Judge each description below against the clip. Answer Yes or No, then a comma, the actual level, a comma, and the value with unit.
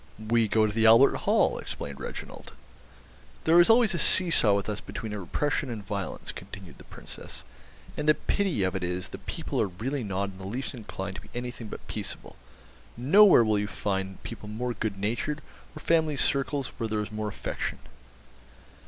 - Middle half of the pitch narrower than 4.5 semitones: No, wide, 5.6 semitones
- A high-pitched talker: No, low, 110 Hz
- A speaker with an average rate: Yes, average, 190 wpm